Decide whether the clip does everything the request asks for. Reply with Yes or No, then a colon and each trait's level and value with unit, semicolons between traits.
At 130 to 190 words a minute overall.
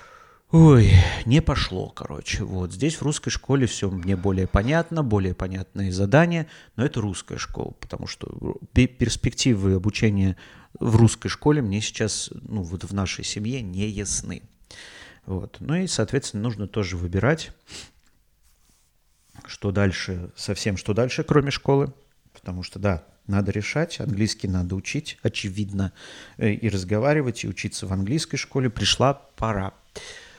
Yes: average, 135 wpm